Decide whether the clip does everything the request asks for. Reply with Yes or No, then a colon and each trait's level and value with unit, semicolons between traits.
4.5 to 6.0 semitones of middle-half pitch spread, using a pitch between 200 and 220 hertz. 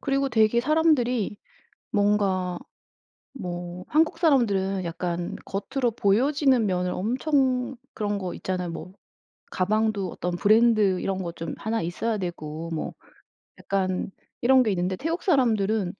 Yes: wide, 5.6 semitones; high, 205 Hz